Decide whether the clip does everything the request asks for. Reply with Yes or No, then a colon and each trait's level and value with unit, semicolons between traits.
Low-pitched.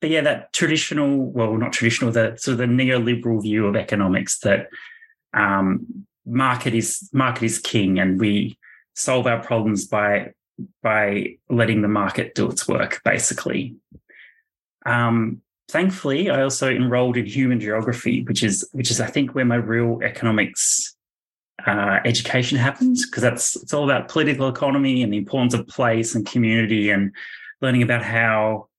Yes: low, 120 Hz